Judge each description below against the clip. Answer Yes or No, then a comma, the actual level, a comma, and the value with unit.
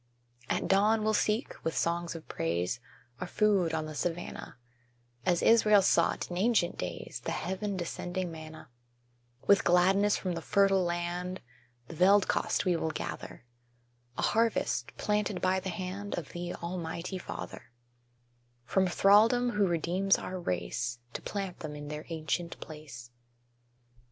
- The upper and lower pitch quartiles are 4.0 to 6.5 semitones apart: No, average, 3.3 semitones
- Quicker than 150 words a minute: No, average, 145 wpm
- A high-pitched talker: No, medium, 180 Hz